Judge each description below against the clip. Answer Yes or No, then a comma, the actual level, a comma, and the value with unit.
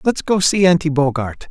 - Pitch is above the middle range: No, medium, 160 Hz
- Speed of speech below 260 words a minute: Yes, average, 200 wpm